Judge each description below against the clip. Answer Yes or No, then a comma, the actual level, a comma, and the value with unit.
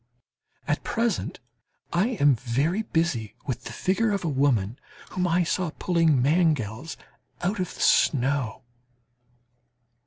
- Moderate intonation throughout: No, wide, 5.9 semitones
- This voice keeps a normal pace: No, slow, 125 wpm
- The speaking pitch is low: No, medium, 160 Hz